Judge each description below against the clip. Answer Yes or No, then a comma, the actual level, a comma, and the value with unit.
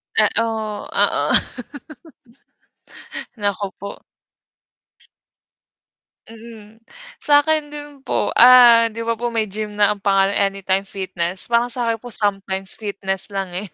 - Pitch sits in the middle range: No, high, 210 Hz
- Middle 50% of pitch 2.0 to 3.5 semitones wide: Yes, average, 3.1 semitones